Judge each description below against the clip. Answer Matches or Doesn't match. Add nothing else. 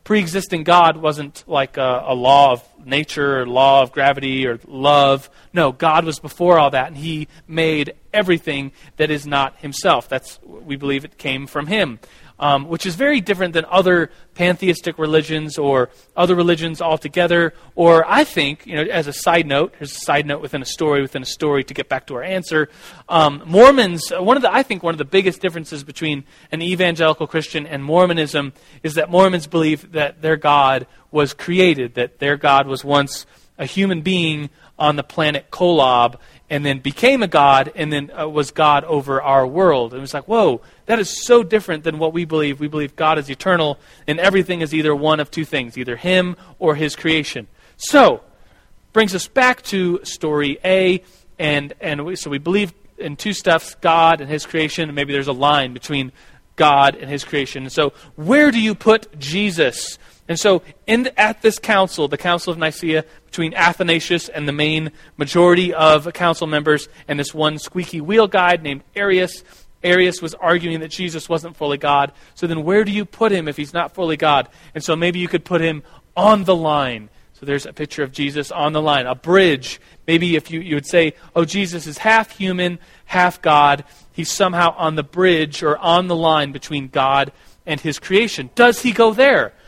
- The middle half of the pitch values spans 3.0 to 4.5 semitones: Matches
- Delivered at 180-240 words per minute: Matches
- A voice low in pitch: Doesn't match